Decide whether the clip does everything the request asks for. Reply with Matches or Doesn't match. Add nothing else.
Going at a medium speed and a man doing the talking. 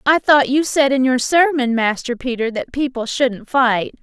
Doesn't match